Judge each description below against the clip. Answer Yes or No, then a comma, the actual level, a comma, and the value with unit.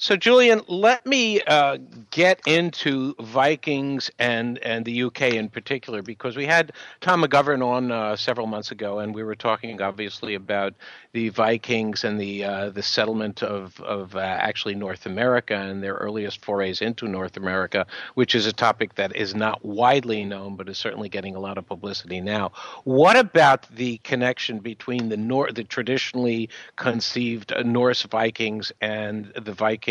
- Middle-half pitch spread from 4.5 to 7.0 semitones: No, average, 3.3 semitones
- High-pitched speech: No, low, 115 Hz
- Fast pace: No, average, 165 wpm